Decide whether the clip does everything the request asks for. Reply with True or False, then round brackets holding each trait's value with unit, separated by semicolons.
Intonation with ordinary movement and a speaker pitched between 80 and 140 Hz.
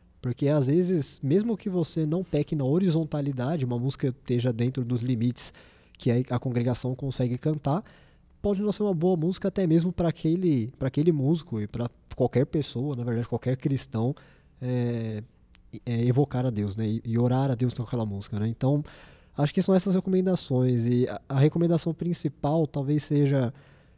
True (5.0 semitones; 135 Hz)